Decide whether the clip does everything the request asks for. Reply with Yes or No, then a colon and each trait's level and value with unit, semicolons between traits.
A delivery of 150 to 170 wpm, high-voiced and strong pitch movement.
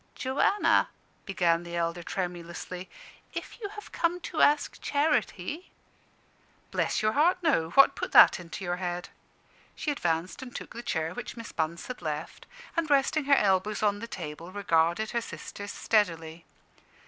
Yes: average, 160 wpm; high, 200 Hz; wide, 8.0 semitones